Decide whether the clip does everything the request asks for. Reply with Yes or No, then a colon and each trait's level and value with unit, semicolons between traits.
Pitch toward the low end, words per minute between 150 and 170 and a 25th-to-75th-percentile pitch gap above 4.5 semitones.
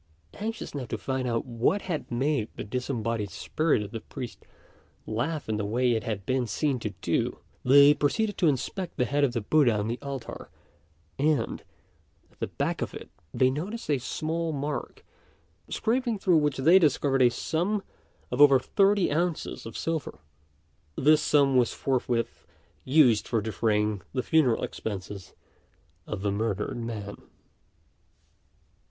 Yes: low, 130 Hz; average, 155 wpm; average, 5.3 semitones